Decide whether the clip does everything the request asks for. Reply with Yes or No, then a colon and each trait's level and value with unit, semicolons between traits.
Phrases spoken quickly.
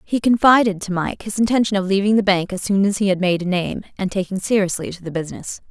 Yes: fast, 250 wpm